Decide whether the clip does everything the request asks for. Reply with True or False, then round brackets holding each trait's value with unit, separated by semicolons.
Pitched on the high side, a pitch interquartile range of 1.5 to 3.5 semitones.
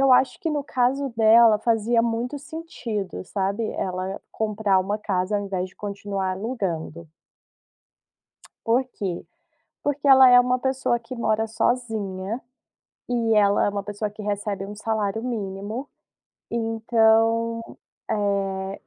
True (220 Hz; 3.2 semitones)